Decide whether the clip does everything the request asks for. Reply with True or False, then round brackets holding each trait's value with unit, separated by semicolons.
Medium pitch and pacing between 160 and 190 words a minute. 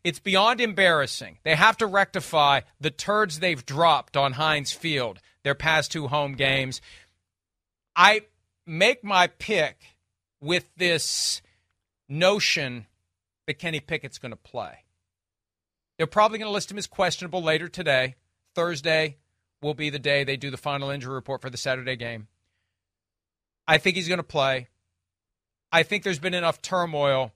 False (145 Hz; 145 wpm)